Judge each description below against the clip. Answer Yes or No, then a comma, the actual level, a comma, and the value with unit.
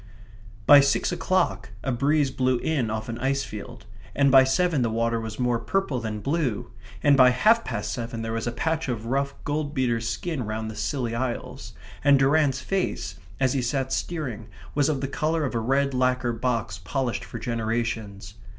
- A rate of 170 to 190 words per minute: Yes, average, 185 wpm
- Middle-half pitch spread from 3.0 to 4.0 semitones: Yes, average, 3.5 semitones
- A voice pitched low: Yes, low, 130 Hz